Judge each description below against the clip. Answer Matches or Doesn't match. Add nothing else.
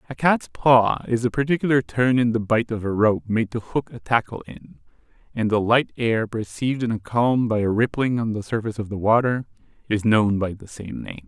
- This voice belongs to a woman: Doesn't match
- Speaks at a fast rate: Matches